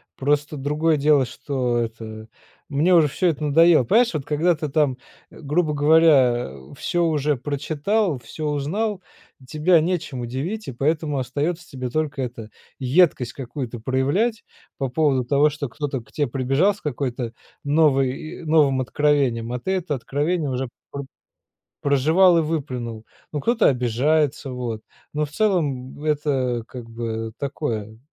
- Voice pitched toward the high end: No, medium, 145 Hz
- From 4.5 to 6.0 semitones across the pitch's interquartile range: No, average, 3.8 semitones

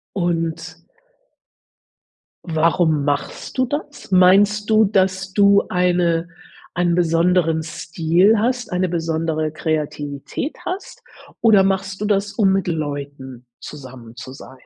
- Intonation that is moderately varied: Yes, average, 3.7 semitones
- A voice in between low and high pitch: Yes, medium, 175 Hz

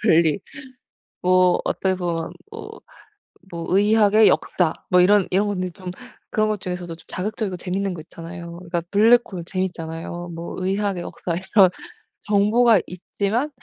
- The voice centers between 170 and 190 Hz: Yes, medium, 185 Hz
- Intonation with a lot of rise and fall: No, average, 2.9 semitones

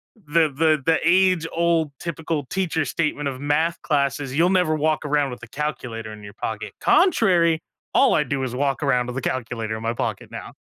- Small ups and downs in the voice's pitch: No, average, 4.0 semitones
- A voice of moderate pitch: Yes, medium, 150 Hz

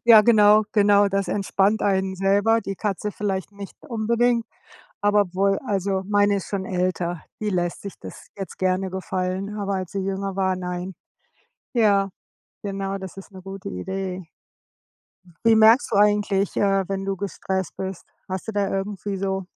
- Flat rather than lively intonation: Yes, narrow, 1.4 semitones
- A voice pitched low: No, high, 195 Hz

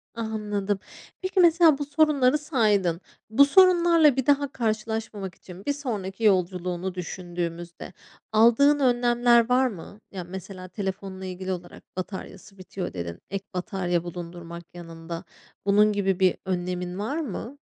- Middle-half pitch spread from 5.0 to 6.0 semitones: Yes, wide, 5.6 semitones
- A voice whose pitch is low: No, high, 200 Hz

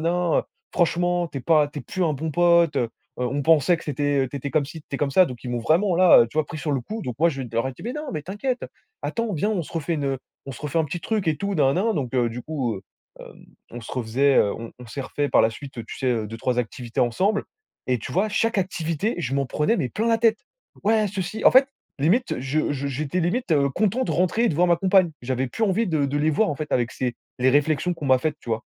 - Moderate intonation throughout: No, wide, 5.7 semitones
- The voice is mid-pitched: Yes, medium, 150 Hz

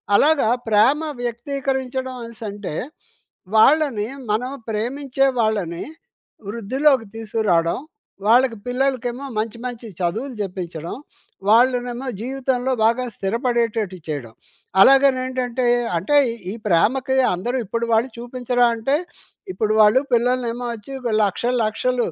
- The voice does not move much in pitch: No, average, 3.2 semitones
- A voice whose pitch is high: Yes, high, 240 Hz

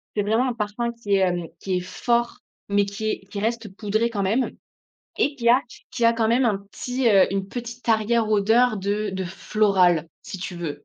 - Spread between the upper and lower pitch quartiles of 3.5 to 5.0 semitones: No, average, 3.1 semitones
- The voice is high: Yes, high, 215 Hz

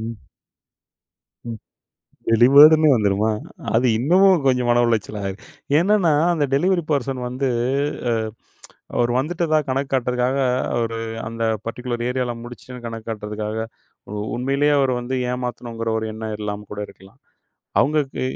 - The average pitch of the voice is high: No, low, 125 Hz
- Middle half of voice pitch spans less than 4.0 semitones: Yes, average, 3.5 semitones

